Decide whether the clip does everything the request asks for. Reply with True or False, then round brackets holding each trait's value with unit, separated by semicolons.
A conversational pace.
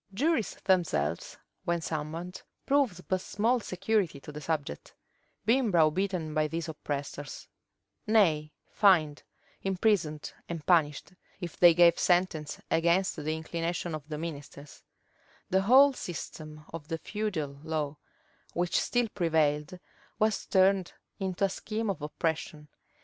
False (125 wpm)